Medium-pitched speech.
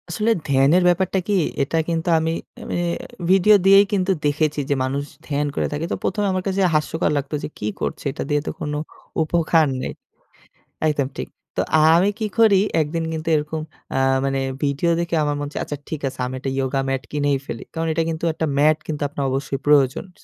Yes: medium, 155 Hz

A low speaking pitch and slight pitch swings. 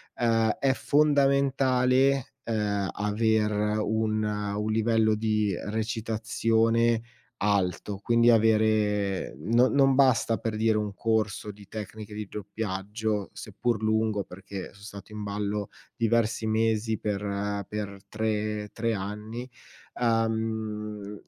Yes: low, 110 Hz; narrow, 1.5 semitones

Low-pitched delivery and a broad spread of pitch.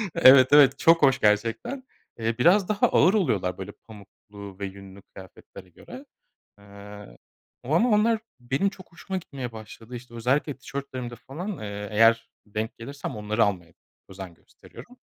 Yes: low, 115 Hz; wide, 6.7 semitones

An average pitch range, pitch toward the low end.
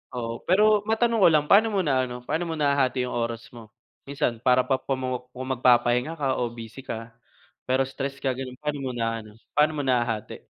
Yes: average, 3.6 semitones; low, 130 Hz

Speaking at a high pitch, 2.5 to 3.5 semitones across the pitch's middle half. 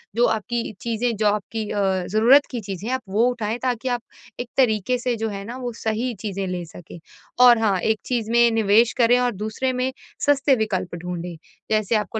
Yes: high, 225 Hz; average, 2.8 semitones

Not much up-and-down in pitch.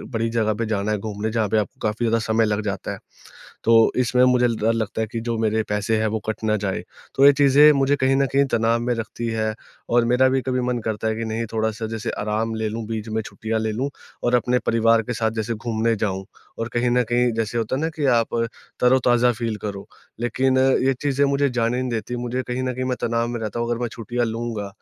Yes: narrow, 2.0 semitones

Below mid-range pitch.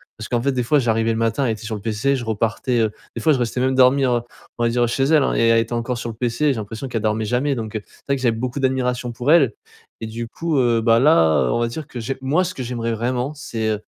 Yes: low, 120 Hz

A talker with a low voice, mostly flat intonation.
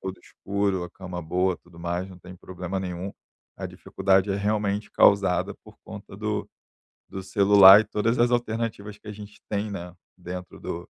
Yes: very low, 95 Hz; narrow, 2.3 semitones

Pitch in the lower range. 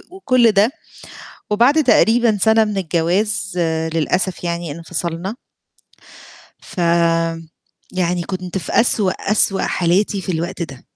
No: high, 190 Hz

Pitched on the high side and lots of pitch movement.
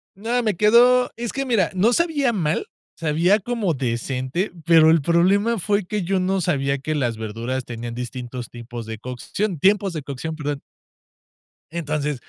No: medium, 165 Hz; wide, 8.0 semitones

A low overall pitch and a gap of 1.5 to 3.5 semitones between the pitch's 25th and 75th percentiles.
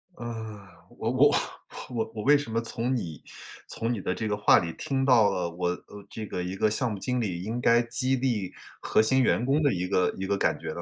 No: low, 110 Hz; average, 4.3 semitones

